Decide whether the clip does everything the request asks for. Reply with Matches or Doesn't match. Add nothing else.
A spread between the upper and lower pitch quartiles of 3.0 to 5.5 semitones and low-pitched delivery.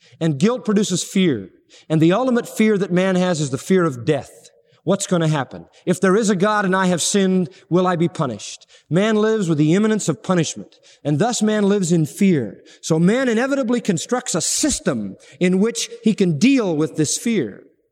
Doesn't match